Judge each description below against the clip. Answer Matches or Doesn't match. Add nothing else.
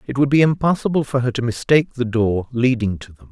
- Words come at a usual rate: Doesn't match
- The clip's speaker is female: Doesn't match